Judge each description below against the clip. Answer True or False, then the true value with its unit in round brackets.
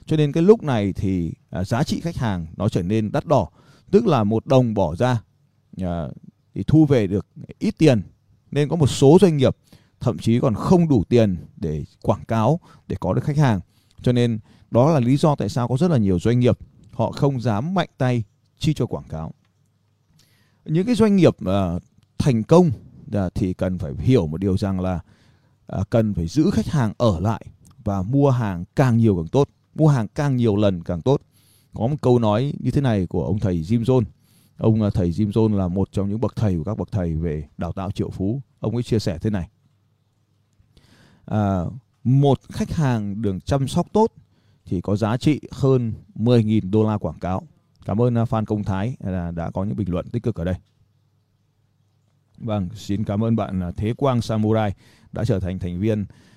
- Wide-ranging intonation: False (4.9 semitones)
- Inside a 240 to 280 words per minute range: False (200 wpm)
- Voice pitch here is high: False (110 Hz)